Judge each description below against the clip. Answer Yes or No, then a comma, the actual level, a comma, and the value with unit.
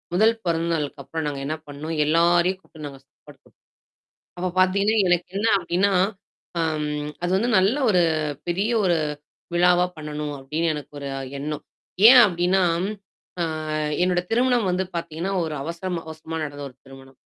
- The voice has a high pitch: No, medium, 170 Hz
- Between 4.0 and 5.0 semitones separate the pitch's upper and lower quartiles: No, average, 3.5 semitones